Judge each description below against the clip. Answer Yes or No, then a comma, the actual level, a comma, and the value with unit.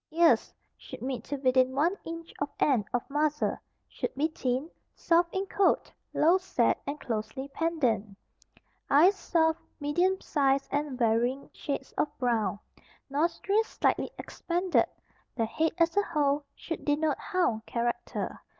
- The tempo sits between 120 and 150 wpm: Yes, average, 140 wpm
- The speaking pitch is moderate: No, very high, 290 Hz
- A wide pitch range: No, average, 4.5 semitones